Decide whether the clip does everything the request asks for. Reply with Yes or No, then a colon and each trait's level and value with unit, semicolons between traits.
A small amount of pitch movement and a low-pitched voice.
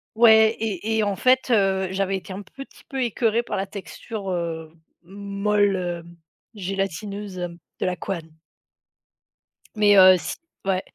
No: narrow, 2.3 semitones; high, 195 Hz